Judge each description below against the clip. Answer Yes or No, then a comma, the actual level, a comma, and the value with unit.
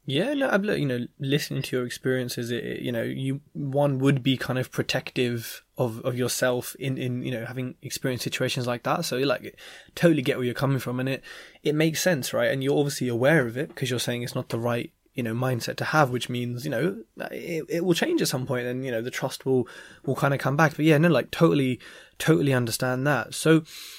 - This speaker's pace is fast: Yes, fast, 240 wpm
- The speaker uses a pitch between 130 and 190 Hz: Yes, low, 135 Hz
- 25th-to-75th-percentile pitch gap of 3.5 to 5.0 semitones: No, average, 3.0 semitones